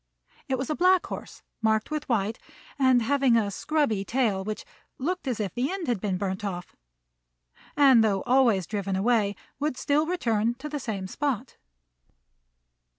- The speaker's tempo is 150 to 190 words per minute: Yes, average, 160 wpm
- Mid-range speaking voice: No, high, 235 Hz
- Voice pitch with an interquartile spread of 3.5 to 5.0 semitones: No, wide, 5.6 semitones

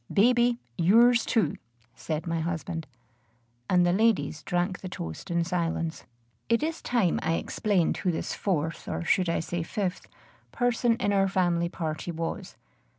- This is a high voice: No, medium, 180 Hz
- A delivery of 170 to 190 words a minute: No, average, 150 wpm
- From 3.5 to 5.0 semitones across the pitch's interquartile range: Yes, average, 4.3 semitones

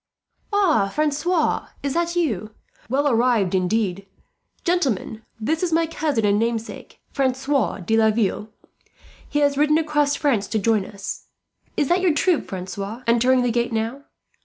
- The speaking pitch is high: Yes, very high, 250 Hz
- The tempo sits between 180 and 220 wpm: No, average, 145 wpm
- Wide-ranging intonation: Yes, wide, 5.7 semitones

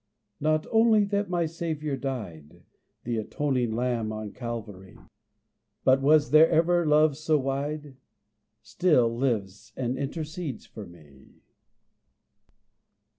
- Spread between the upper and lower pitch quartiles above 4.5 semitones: Yes, wide, 5.6 semitones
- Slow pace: Yes, slow, 110 wpm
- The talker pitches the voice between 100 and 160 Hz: Yes, low, 135 Hz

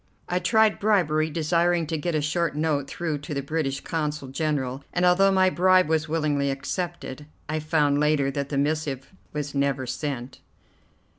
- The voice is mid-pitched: Yes, medium, 150 Hz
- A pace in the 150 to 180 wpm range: Yes, average, 165 wpm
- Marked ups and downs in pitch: No, average, 3.2 semitones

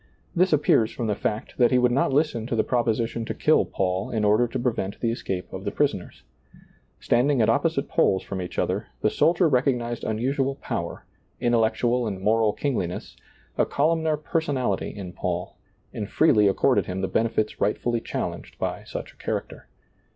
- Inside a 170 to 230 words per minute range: Yes, average, 175 wpm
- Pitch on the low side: Yes, low, 120 Hz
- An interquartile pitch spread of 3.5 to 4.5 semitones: Yes, average, 4.2 semitones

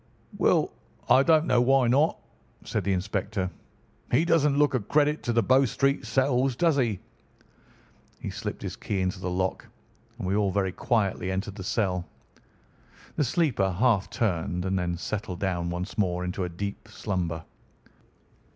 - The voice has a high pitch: No, low, 100 Hz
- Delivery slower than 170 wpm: Yes, average, 160 wpm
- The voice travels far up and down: Yes, wide, 5.9 semitones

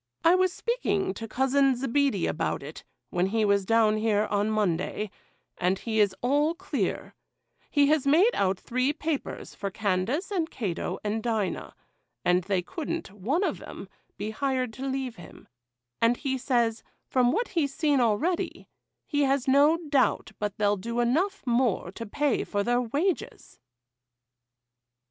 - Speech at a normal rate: Yes, average, 155 wpm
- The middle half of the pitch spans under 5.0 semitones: No, wide, 5.6 semitones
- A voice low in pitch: No, high, 245 Hz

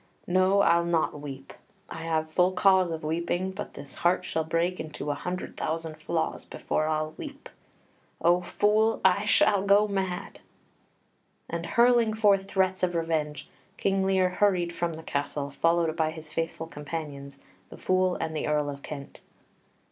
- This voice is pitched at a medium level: Yes, medium, 170 Hz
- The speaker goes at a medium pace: Yes, average, 160 wpm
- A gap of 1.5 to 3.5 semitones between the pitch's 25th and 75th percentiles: Yes, average, 3.2 semitones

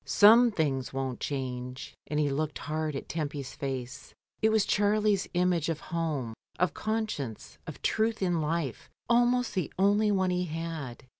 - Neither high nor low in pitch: Yes, medium, 165 Hz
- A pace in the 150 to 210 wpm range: Yes, average, 155 wpm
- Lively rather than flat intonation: Yes, wide, 6.6 semitones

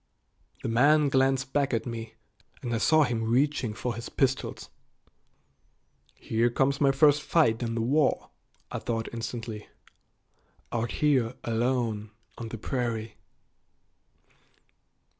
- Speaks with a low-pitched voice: Yes, low, 120 Hz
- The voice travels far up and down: No, average, 3.0 semitones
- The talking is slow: Yes, slow, 120 wpm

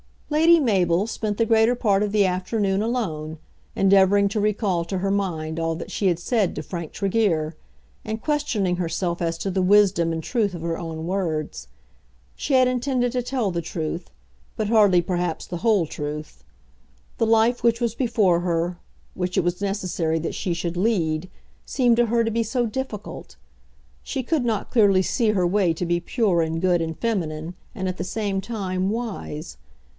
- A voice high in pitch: Yes, high, 195 Hz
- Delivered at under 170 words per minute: No, average, 180 wpm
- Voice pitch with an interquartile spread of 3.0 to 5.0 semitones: Yes, average, 4.7 semitones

